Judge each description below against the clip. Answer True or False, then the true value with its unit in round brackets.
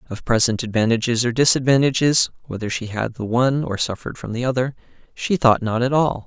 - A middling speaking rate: True (170 wpm)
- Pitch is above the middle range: False (120 Hz)